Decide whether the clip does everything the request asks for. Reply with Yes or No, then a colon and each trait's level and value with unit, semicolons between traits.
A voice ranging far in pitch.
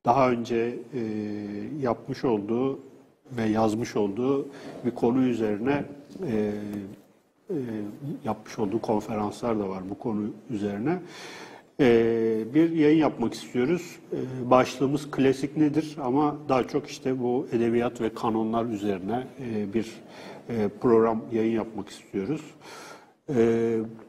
No: average, 3.1 semitones